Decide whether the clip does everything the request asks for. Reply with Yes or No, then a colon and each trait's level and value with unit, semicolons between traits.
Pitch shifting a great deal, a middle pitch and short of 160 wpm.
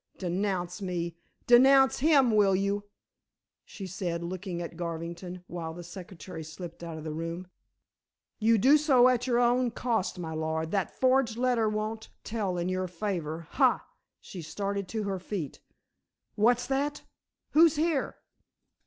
No: wide, 5.8 semitones; high, 195 Hz; average, 145 wpm